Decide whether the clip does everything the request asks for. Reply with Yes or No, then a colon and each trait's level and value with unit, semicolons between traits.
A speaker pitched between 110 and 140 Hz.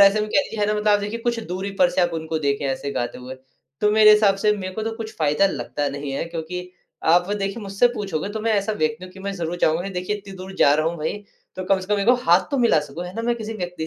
No: high, 190 Hz